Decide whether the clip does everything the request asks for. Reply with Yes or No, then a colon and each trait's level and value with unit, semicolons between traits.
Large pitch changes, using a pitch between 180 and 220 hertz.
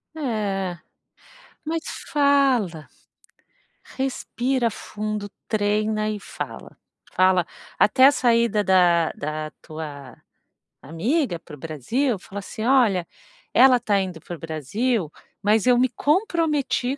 Yes: wide, 6.5 semitones; high, 215 Hz